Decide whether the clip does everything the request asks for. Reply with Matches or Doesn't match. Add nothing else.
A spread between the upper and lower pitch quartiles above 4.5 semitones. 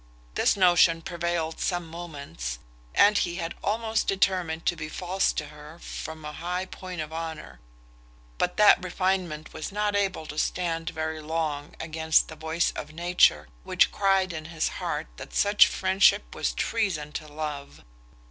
Doesn't match